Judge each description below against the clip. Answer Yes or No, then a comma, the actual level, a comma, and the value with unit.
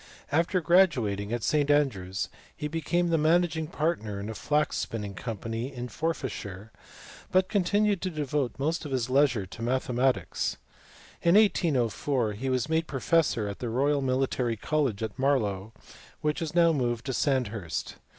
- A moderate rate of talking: Yes, average, 150 wpm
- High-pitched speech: No, low, 135 Hz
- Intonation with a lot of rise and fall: Yes, wide, 6.0 semitones